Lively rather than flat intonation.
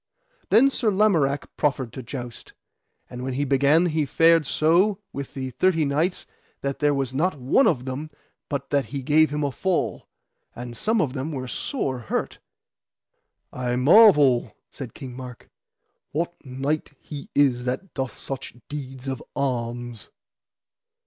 No: average, 3.5 semitones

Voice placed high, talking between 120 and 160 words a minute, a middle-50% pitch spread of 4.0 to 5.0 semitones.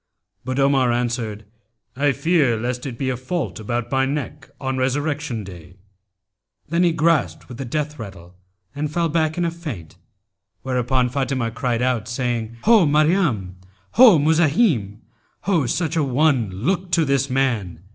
No: low, 135 Hz; average, 155 wpm; average, 4.6 semitones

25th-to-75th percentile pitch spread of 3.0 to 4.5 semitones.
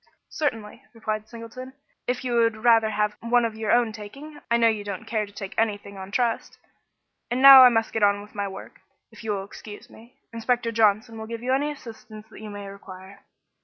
No: narrow, 2.5 semitones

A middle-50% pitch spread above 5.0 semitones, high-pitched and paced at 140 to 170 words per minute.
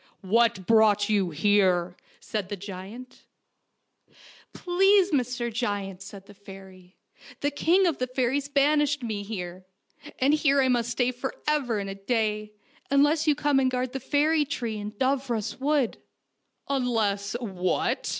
Yes: wide, 5.5 semitones; high, 235 Hz; average, 160 wpm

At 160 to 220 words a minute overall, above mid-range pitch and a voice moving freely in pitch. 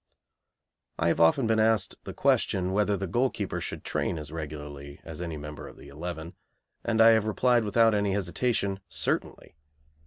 No: average, 165 wpm; very low, 95 Hz; wide, 5.9 semitones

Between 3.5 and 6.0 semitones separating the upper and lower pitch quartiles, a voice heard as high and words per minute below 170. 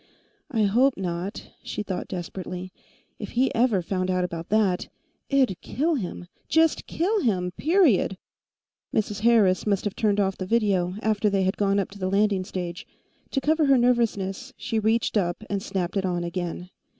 No: average, 4.1 semitones; high, 200 Hz; average, 175 wpm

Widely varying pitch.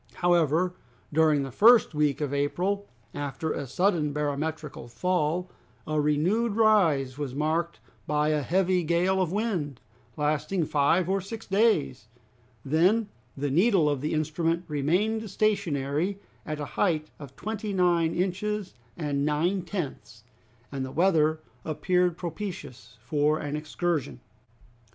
No: average, 4.2 semitones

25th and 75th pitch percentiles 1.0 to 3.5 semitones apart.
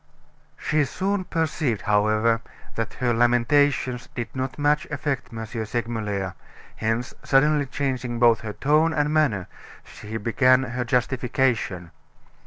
No: average, 4.2 semitones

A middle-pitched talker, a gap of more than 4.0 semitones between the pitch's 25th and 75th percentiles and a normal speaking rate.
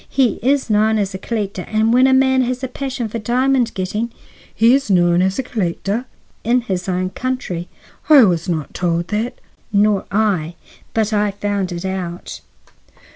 No: high, 210 Hz; average, 4.9 semitones; average, 175 wpm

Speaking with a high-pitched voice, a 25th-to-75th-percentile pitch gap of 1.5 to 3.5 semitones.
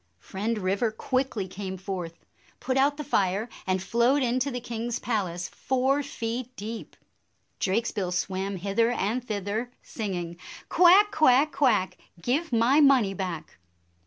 No: high, 225 Hz; average, 5.1 semitones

